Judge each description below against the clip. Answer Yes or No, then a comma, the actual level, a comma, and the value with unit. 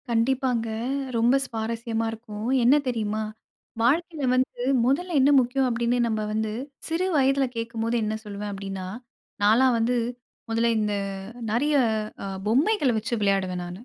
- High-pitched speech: Yes, high, 230 Hz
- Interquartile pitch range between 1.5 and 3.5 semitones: Yes, average, 3.2 semitones